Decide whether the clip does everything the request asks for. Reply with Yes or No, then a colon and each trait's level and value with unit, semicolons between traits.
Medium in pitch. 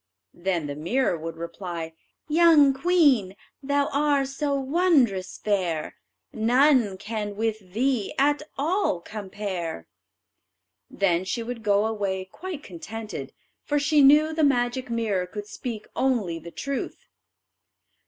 No: high, 225 Hz